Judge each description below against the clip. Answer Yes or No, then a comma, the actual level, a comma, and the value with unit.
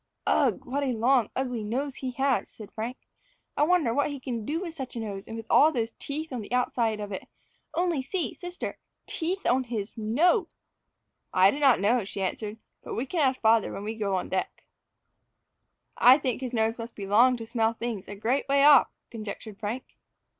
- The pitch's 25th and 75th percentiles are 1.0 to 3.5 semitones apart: No, average, 4.1 semitones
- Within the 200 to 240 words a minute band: Yes, fast, 205 wpm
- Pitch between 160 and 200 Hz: No, high, 240 Hz